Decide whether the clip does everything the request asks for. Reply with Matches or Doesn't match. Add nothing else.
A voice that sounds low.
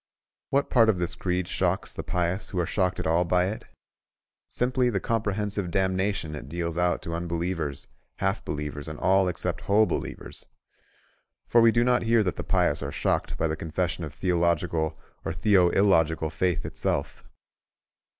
Matches